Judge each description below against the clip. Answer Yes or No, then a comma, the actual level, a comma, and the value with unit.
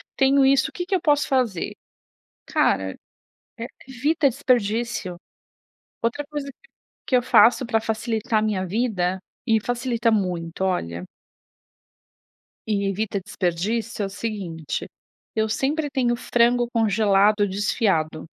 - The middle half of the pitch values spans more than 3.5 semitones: Yes, average, 4.2 semitones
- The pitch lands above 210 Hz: Yes, high, 225 Hz